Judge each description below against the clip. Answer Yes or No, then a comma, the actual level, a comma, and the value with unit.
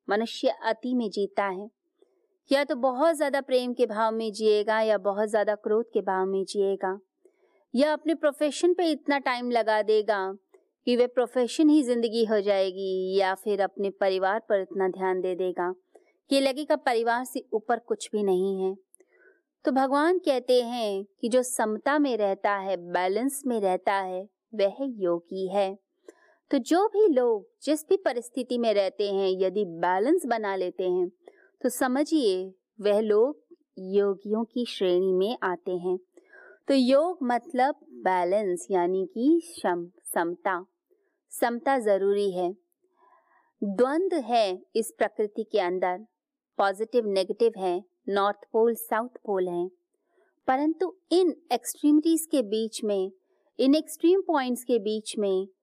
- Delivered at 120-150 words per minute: Yes, average, 145 wpm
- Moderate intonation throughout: No, wide, 6.9 semitones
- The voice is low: No, high, 225 Hz